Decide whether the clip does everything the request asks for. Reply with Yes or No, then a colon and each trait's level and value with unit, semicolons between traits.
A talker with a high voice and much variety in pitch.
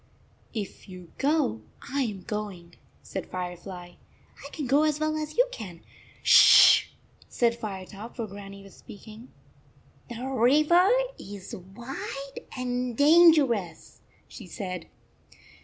Yes: high, 225 Hz; wide, 6.4 semitones